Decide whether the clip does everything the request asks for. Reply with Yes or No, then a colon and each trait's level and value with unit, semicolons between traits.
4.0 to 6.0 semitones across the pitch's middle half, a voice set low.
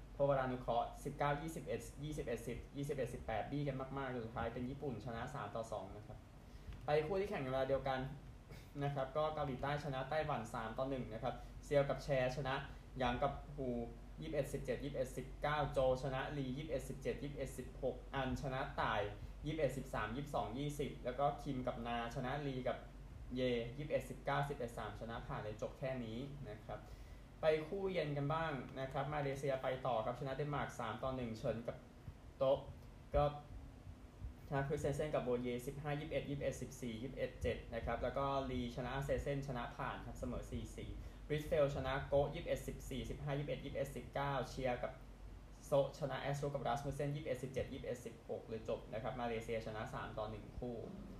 No: average, 2.8 semitones; low, 130 Hz